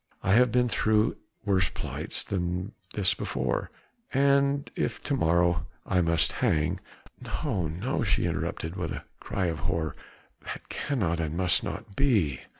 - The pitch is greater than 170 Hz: No, very low, 95 Hz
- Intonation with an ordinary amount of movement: No, wide, 5.7 semitones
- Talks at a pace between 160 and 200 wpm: No, average, 150 wpm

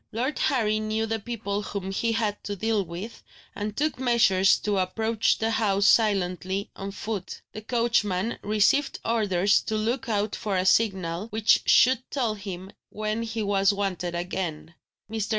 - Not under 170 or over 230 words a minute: No, average, 160 wpm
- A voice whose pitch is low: No, high, 210 Hz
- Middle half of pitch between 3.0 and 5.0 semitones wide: No, narrow, 2.5 semitones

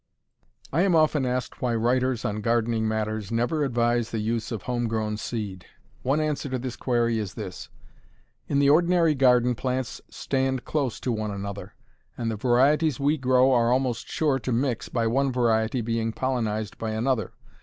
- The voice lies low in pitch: Yes, low, 120 Hz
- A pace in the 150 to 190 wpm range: Yes, average, 175 wpm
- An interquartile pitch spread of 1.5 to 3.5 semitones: Yes, average, 2.9 semitones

